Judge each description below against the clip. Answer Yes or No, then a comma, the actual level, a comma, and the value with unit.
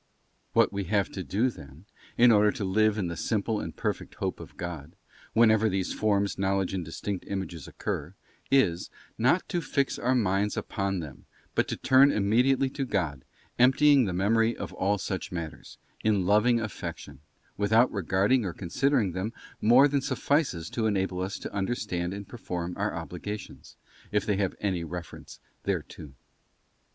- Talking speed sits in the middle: Yes, average, 165 wpm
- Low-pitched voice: Yes, low, 100 Hz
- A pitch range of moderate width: Yes, average, 4.0 semitones